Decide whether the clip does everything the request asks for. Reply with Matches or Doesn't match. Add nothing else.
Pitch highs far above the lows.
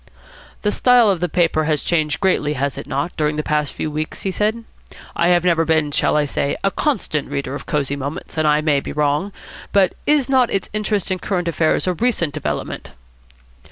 Doesn't match